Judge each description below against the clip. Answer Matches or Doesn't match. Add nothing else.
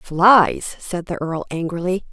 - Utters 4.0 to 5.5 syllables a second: Doesn't match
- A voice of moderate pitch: Matches